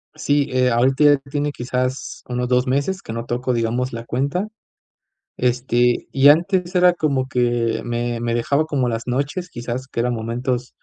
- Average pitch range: Yes, average, 3.0 semitones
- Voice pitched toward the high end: No, low, 125 Hz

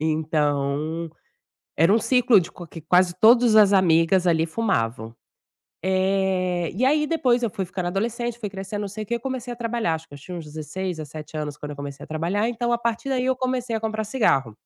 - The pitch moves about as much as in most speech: No, wide, 6.5 semitones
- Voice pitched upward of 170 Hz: Yes, high, 190 Hz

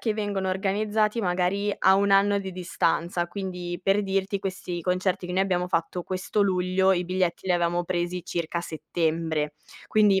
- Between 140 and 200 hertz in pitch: Yes, medium, 185 Hz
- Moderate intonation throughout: No, narrow, 2.0 semitones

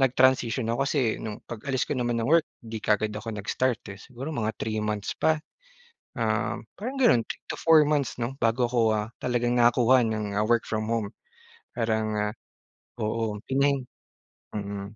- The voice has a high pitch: No, low, 115 Hz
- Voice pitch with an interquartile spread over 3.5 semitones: No, average, 3.2 semitones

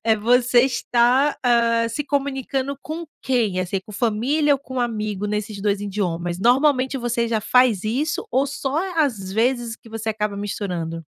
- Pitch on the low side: No, high, 235 Hz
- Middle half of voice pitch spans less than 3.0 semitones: No, average, 4.1 semitones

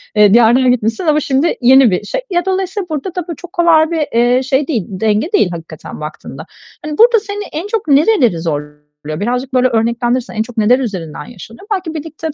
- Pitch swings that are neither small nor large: No, wide, 6.8 semitones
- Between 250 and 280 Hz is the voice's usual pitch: Yes, very high, 260 Hz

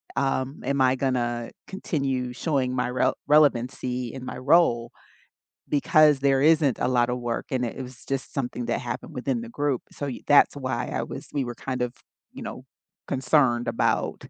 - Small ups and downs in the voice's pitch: Yes, narrow, 2.2 semitones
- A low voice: Yes, low, 130 Hz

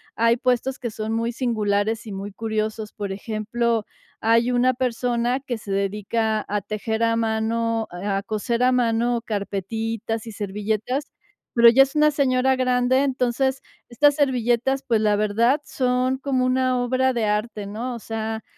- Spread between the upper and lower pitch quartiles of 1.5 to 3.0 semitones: Yes, average, 2.7 semitones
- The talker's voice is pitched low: No, high, 230 Hz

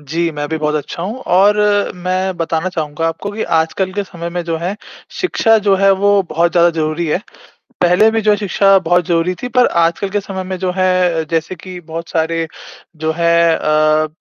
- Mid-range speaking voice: Yes, medium, 175 Hz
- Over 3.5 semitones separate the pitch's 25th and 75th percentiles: No, average, 2.8 semitones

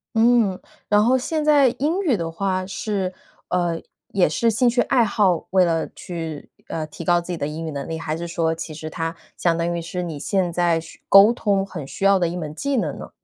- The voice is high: No, medium, 180 Hz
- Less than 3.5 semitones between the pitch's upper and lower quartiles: No, average, 4.2 semitones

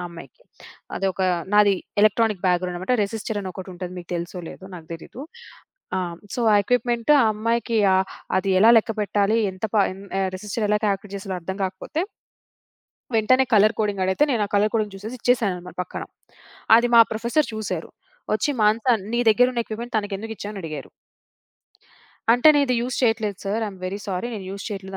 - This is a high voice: Yes, high, 210 Hz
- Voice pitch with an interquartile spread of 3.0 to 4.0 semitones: Yes, average, 3.3 semitones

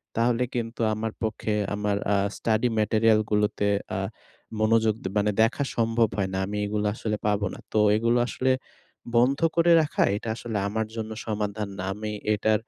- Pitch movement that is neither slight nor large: No, narrow, 1.7 semitones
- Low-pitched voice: Yes, low, 110 Hz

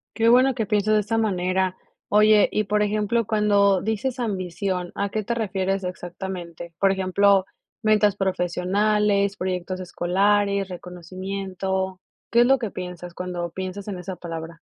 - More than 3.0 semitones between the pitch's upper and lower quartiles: No, narrow, 2.5 semitones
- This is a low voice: No, high, 195 Hz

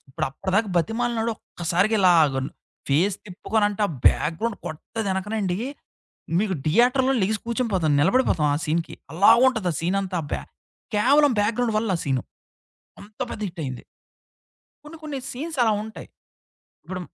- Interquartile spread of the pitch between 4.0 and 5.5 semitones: Yes, average, 5.1 semitones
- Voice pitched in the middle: No, high, 205 Hz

